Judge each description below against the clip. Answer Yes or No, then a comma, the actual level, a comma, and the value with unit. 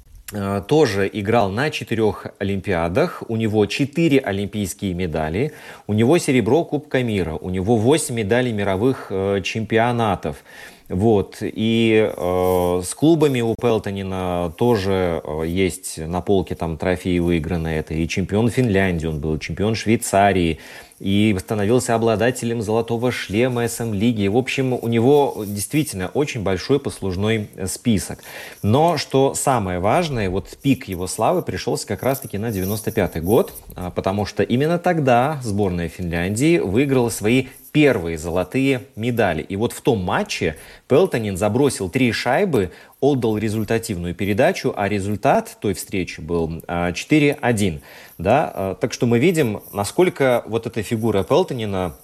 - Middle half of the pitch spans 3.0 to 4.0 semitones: No, average, 4.8 semitones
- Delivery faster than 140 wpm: No, average, 130 wpm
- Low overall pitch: Yes, low, 105 Hz